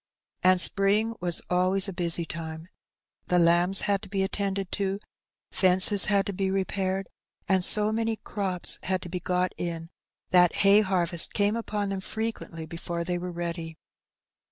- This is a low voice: No, medium, 185 Hz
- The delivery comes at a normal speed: Yes, average, 170 wpm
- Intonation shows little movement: Yes, narrow, 2.2 semitones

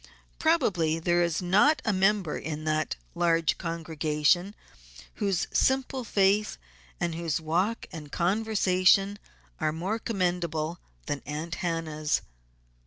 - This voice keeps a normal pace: No, slow, 110 wpm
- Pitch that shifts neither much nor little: Yes, average, 3.9 semitones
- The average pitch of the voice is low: No, medium, 175 Hz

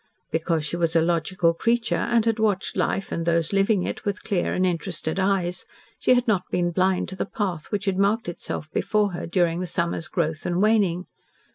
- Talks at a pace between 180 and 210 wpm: Yes, fast, 205 wpm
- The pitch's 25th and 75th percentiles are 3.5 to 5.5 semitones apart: No, average, 3.0 semitones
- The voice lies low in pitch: No, medium, 185 Hz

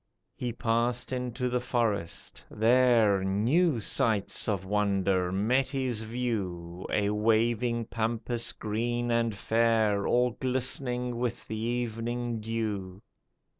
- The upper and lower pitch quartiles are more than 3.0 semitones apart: No, average, 2.7 semitones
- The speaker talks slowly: Yes, slow, 110 wpm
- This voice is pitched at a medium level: No, low, 115 Hz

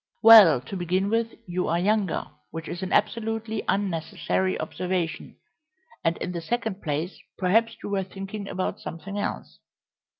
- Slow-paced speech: No, average, 145 wpm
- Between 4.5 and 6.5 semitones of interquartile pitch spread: No, average, 3.6 semitones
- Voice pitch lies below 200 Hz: Yes, high, 190 Hz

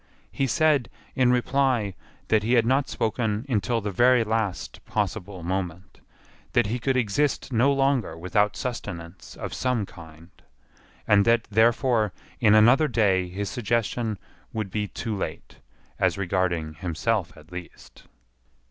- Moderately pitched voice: No, low, 110 Hz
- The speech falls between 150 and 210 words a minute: No, average, 140 wpm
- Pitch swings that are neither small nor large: Yes, average, 4.6 semitones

